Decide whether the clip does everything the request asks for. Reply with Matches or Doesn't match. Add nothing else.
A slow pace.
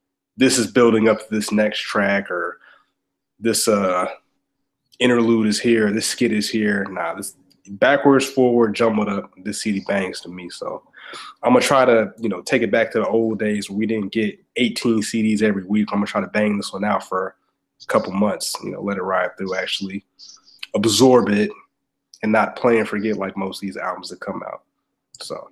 Doesn't match